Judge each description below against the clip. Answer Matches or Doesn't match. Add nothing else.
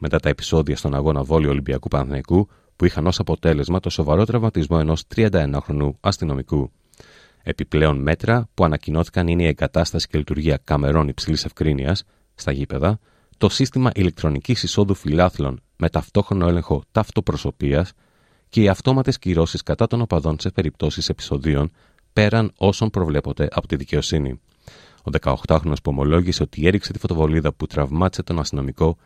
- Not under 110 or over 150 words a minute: Matches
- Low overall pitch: Matches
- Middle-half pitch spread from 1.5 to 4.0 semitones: Doesn't match